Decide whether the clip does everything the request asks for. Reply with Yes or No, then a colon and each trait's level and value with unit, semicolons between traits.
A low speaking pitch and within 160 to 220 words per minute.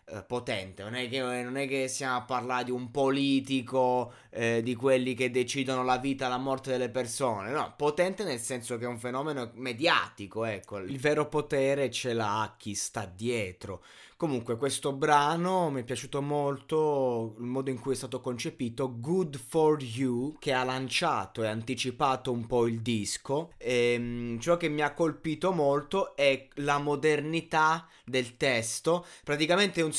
Yes: low, 130 Hz; fast, 170 wpm